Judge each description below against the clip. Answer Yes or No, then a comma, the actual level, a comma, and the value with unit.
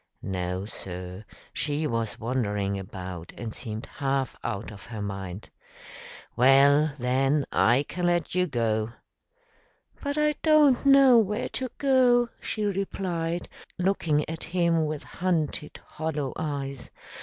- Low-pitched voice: No, medium, 145 Hz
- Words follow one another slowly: Yes, slow, 125 wpm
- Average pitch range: No, wide, 8.5 semitones